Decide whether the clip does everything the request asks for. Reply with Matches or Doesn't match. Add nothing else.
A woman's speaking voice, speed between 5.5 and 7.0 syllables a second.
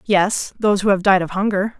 Matches